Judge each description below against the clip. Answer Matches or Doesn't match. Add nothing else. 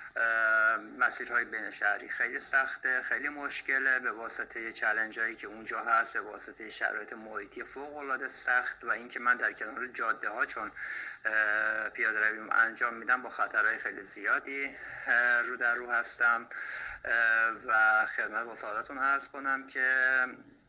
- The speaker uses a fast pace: Doesn't match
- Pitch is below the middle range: Matches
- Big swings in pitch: Doesn't match